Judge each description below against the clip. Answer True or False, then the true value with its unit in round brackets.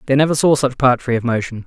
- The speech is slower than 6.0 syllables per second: False (6.6 syllables/s)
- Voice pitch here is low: True (130 Hz)